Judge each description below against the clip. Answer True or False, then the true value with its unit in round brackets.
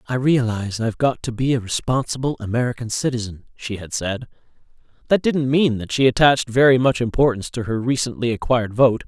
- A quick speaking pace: False (180 wpm)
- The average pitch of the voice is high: False (120 Hz)